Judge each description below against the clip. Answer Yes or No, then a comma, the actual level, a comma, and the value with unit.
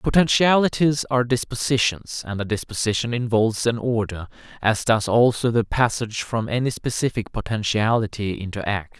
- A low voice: Yes, low, 115 Hz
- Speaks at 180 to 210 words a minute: No, slow, 135 wpm